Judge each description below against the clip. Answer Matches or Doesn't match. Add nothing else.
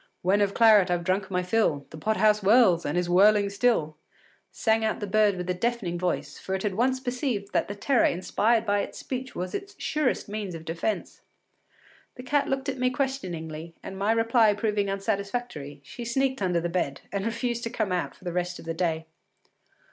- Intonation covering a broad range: Doesn't match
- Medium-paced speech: Doesn't match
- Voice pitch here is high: Matches